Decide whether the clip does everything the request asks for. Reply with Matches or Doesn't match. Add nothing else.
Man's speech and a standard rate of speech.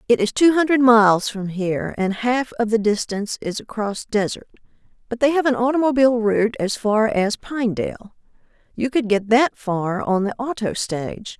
Doesn't match